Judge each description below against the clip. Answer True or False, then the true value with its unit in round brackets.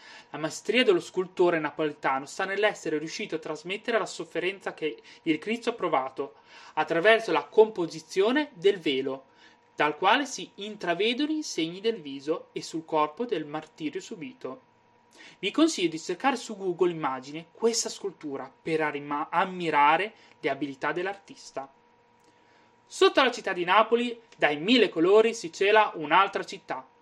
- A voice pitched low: False (195 Hz)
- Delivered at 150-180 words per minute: False (140 wpm)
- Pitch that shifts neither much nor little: False (6.3 semitones)